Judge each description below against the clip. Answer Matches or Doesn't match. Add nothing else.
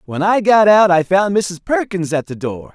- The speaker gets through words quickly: Matches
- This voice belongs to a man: Matches